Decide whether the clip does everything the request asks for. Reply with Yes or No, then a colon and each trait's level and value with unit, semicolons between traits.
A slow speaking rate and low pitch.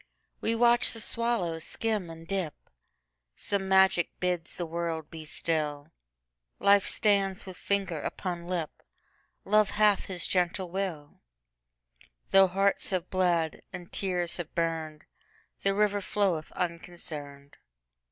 No: slow, 105 wpm; medium, 175 Hz